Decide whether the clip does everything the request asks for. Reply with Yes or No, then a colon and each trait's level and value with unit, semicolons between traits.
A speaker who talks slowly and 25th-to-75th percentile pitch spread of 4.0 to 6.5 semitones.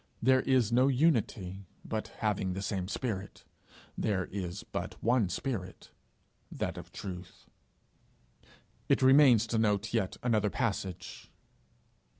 Yes: slow, 120 wpm; average, 4.3 semitones